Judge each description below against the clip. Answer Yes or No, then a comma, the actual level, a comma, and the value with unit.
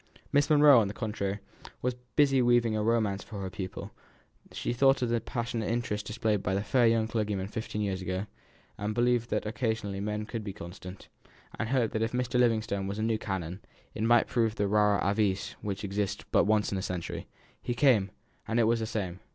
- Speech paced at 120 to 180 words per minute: No, fast, 205 wpm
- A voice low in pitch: Yes, low, 110 Hz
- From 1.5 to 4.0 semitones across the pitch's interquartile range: Yes, average, 2.9 semitones